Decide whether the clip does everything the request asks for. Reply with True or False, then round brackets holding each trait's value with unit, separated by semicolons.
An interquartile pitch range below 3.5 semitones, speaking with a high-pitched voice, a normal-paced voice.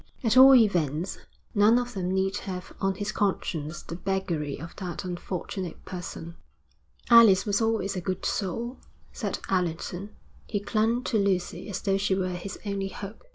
True (2.6 semitones; 195 Hz; 160 wpm)